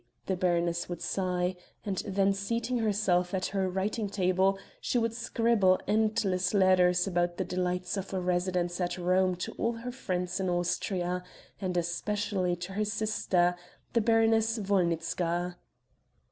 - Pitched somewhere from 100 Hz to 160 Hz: No, medium, 185 Hz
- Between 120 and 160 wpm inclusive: Yes, average, 145 wpm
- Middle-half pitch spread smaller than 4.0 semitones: Yes, average, 2.7 semitones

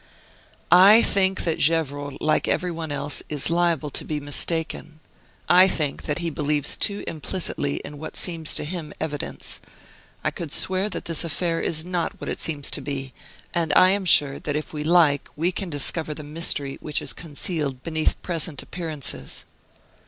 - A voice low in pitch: No, medium, 160 Hz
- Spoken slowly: No, average, 175 wpm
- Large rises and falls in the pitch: No, average, 2.9 semitones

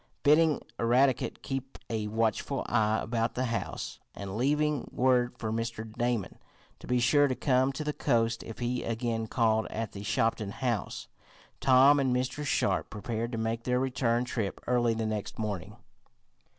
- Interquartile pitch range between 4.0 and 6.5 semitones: No, narrow, 2.6 semitones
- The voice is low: Yes, low, 120 Hz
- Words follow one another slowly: No, average, 165 wpm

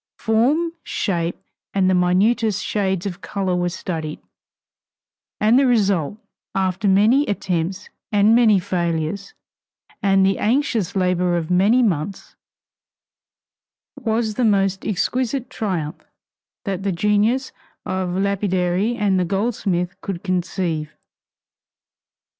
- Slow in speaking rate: Yes, slow, 115 wpm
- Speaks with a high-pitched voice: Yes, high, 195 Hz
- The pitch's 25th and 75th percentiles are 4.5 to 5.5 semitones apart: No, average, 3.3 semitones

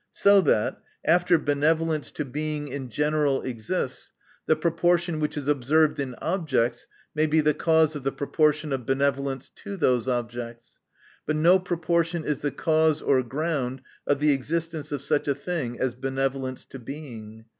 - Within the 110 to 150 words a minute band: No, average, 160 wpm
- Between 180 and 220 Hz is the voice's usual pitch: No, medium, 145 Hz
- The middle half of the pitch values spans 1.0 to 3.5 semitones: Yes, average, 3.2 semitones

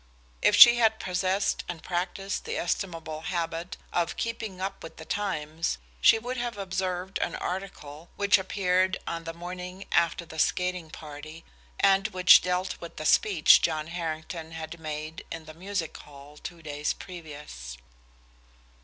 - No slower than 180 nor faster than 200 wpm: No, average, 150 wpm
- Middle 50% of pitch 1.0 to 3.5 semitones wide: Yes, average, 3.2 semitones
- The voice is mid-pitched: Yes, medium, 175 Hz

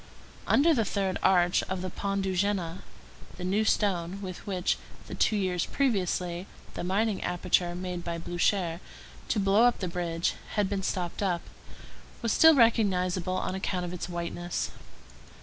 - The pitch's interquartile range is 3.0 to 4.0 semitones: No, narrow, 2.4 semitones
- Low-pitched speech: No, medium, 185 Hz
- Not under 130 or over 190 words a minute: Yes, average, 160 wpm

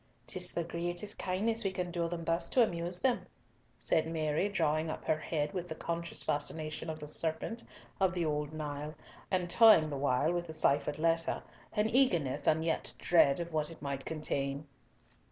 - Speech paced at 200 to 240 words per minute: No, average, 180 wpm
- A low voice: No, medium, 165 Hz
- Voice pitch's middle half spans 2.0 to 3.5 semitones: Yes, narrow, 2.5 semitones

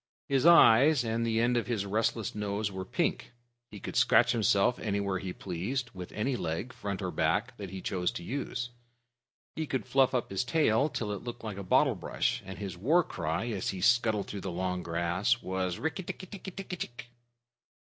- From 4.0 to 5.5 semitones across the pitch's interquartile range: Yes, average, 4.6 semitones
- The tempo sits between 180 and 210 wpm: Yes, average, 200 wpm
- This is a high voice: No, low, 105 Hz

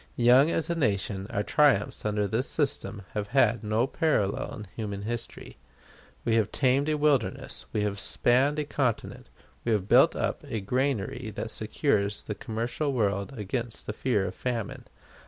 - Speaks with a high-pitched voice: No, low, 115 Hz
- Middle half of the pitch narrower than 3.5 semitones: No, average, 4.5 semitones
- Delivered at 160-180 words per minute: Yes, average, 165 wpm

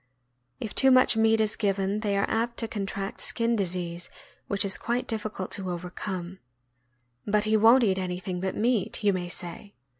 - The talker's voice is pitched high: Yes, high, 200 Hz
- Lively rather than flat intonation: No, average, 3.1 semitones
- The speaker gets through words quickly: No, average, 175 wpm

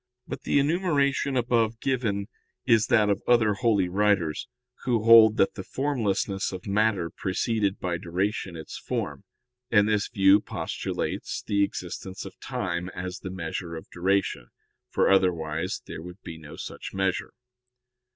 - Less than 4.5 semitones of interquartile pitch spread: Yes, average, 3.7 semitones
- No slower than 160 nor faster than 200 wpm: No, average, 145 wpm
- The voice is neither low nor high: No, low, 100 Hz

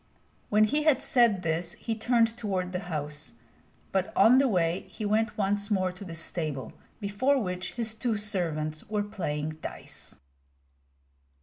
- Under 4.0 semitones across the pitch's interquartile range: No, average, 4.7 semitones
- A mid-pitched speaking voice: No, high, 200 Hz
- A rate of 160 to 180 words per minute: No, average, 150 wpm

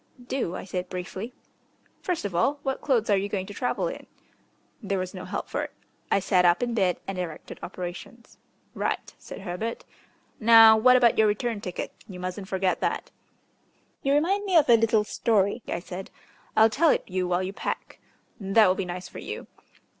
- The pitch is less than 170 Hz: No, high, 205 Hz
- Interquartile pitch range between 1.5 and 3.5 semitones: No, average, 4.2 semitones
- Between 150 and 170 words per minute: No, average, 190 wpm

